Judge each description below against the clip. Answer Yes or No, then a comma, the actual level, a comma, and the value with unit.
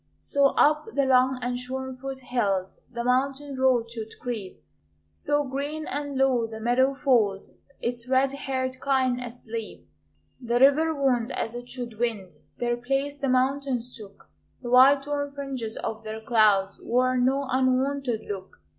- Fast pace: No, average, 155 wpm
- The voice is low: No, very high, 255 Hz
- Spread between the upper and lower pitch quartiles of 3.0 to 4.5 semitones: No, narrow, 2.6 semitones